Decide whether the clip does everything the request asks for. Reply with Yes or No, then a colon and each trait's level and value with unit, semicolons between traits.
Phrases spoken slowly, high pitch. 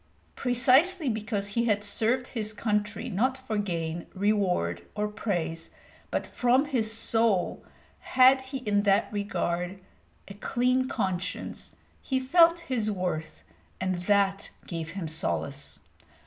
Yes: slow, 125 wpm; high, 210 Hz